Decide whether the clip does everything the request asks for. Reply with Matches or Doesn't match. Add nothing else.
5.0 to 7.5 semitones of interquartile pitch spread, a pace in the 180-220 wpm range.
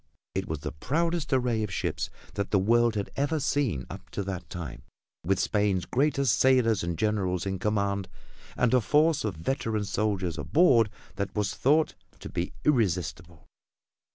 Doesn't match